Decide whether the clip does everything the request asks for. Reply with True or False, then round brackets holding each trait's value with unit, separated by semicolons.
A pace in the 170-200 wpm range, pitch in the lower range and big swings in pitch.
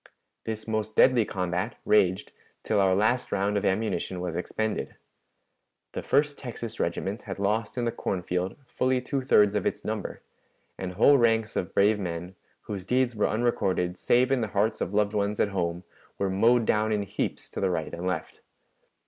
False (180 wpm; 105 Hz; 3.3 semitones)